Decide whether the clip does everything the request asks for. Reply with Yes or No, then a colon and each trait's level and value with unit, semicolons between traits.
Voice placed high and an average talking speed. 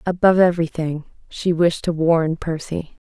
No: medium, 165 Hz; average, 155 wpm